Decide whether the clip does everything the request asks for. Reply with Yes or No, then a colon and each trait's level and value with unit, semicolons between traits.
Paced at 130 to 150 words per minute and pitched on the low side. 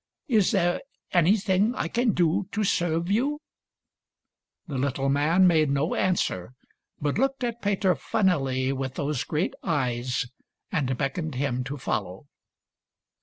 No: average, 140 wpm; medium, 160 Hz